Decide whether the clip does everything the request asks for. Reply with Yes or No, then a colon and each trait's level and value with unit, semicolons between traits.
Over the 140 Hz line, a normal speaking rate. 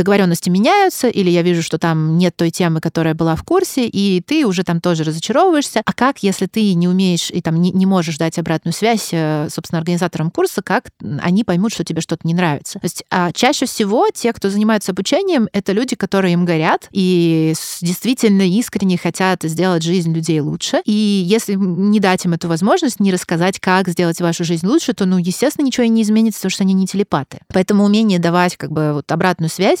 No: medium, 185 Hz; fast, 205 wpm